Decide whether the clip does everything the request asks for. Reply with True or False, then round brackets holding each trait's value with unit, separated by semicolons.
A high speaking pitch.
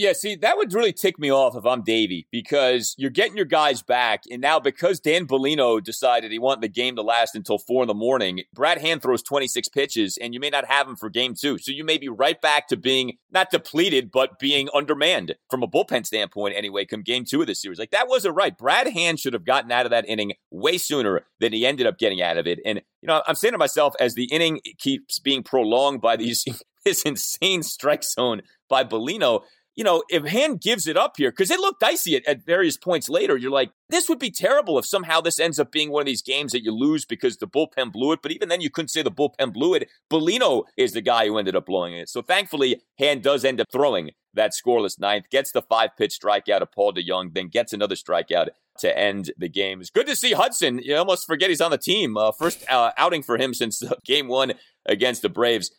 False (140 Hz)